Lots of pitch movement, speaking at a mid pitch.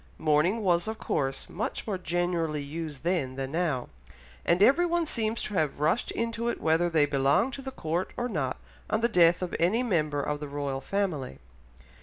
Yes: wide, 6.4 semitones; medium, 170 Hz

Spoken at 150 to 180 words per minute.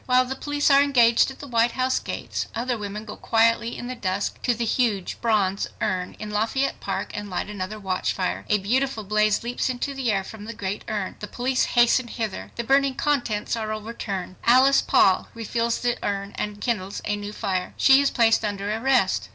No: average, 200 wpm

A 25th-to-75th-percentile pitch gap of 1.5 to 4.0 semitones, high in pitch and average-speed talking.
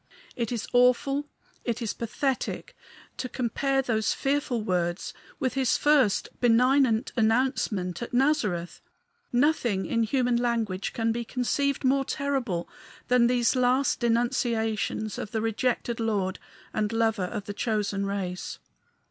No: average, 3.2 semitones; high, 235 Hz; slow, 130 wpm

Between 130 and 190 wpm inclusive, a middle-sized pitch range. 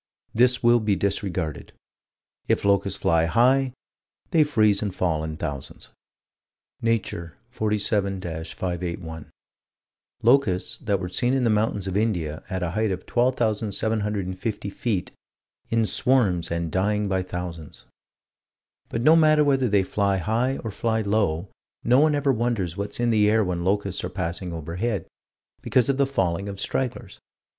Yes: average, 145 wpm; average, 4.6 semitones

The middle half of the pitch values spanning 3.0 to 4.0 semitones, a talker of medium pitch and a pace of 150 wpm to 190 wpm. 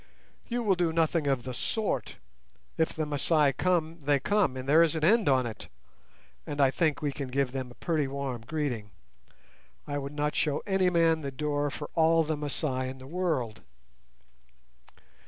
Yes: average, 3.4 semitones; medium, 150 Hz; average, 180 wpm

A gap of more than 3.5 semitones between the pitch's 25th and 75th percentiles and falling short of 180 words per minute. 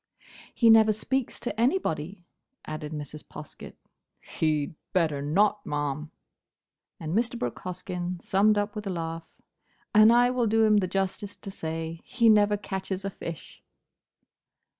Yes: average, 5.0 semitones; average, 140 wpm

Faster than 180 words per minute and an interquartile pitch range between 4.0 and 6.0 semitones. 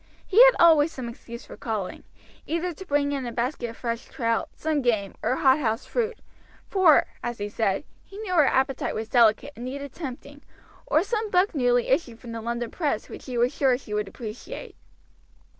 Yes: average, 190 wpm; average, 5.0 semitones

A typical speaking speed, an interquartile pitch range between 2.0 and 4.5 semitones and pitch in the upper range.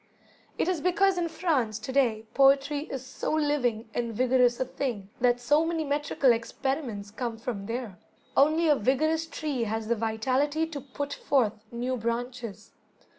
Yes: average, 160 wpm; average, 4.2 semitones; very high, 260 Hz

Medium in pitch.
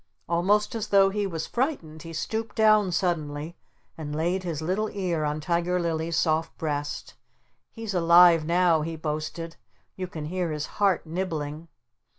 Yes: medium, 170 Hz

